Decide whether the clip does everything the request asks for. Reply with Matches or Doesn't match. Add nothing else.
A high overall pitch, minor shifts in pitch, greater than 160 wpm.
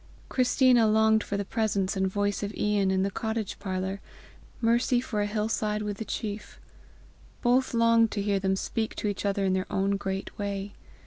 Matches